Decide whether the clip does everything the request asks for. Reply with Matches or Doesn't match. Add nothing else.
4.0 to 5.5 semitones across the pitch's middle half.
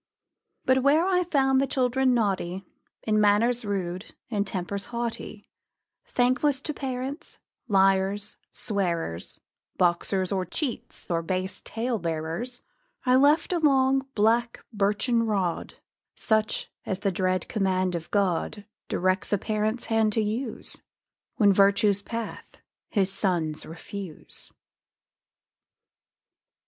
Matches